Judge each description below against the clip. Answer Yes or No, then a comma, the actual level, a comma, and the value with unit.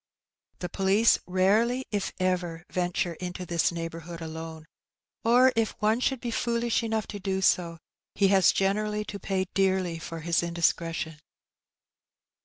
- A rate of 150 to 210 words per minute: No, average, 140 wpm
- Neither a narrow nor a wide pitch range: Yes, average, 3.8 semitones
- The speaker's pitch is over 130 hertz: Yes, medium, 185 Hz